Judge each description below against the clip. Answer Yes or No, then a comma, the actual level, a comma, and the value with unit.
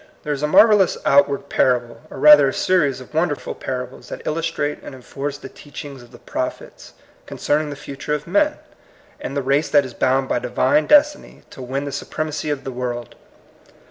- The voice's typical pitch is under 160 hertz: Yes, medium, 140 Hz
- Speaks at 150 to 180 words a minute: No, average, 195 wpm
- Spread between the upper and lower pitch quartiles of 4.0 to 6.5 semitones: No, narrow, 2.6 semitones